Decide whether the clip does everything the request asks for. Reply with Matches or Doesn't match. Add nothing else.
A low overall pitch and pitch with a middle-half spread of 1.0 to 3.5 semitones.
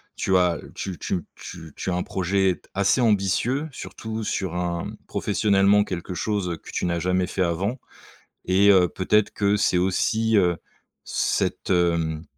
Matches